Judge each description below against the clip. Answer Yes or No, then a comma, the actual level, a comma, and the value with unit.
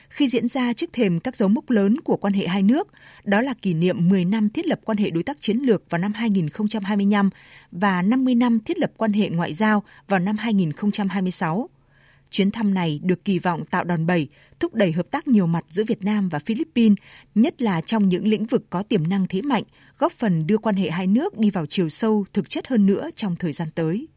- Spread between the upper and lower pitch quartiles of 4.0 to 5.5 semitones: No, average, 3.6 semitones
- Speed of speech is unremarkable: Yes, average, 230 wpm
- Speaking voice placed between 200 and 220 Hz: Yes, high, 205 Hz